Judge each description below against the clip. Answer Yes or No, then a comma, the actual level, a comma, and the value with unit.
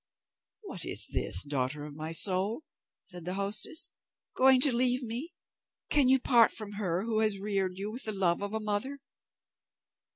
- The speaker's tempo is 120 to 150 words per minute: No, average, 170 wpm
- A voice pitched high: Yes, high, 205 Hz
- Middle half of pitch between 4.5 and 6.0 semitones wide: Yes, average, 4.9 semitones